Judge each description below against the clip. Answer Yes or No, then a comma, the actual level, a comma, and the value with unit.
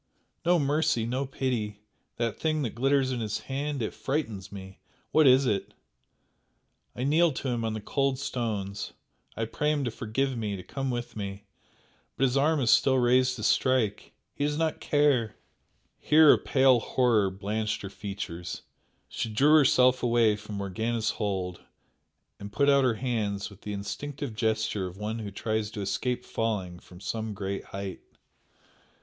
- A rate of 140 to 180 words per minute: Yes, average, 170 wpm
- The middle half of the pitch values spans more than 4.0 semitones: Yes, average, 4.5 semitones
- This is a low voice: Yes, low, 115 Hz